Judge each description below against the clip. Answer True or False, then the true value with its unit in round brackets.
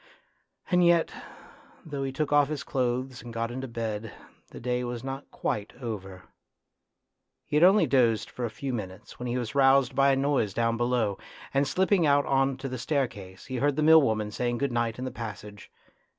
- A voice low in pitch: True (125 Hz)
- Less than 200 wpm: False (205 wpm)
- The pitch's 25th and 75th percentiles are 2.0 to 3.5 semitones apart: True (3.2 semitones)